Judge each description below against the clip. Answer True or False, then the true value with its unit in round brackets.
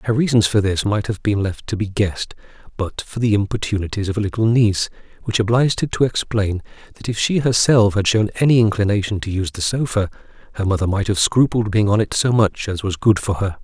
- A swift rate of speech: True (225 wpm)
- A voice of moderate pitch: False (105 Hz)